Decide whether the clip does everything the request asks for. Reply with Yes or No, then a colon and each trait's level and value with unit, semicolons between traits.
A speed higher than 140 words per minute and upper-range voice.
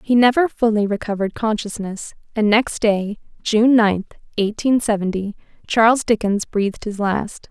No: slow, 135 wpm; high, 215 Hz